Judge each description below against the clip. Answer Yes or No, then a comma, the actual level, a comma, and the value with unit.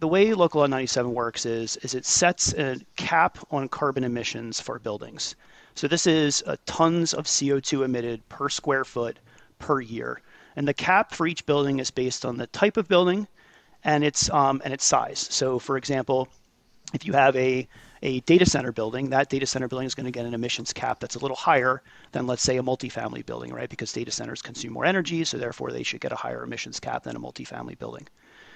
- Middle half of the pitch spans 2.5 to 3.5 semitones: Yes, average, 3.2 semitones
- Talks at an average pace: No, fast, 210 wpm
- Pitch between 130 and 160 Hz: Yes, low, 135 Hz